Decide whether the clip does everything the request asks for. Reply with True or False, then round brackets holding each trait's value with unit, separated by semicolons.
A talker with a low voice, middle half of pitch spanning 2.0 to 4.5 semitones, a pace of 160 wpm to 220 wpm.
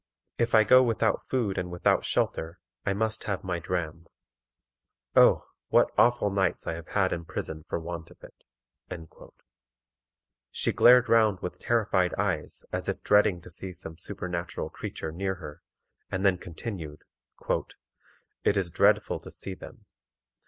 False (95 Hz; 3.5 semitones; 150 wpm)